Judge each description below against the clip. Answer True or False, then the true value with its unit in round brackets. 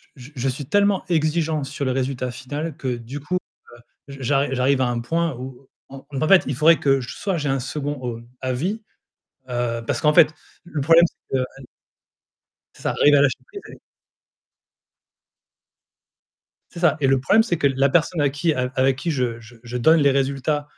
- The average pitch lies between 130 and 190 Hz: True (140 Hz)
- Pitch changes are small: False (3.4 semitones)